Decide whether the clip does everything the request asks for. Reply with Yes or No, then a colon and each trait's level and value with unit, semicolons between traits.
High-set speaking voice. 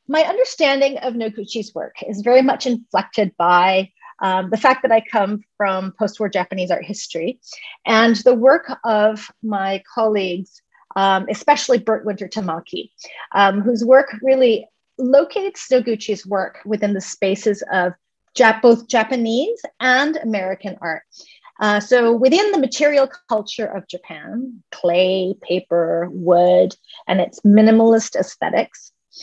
Yes: high, 220 Hz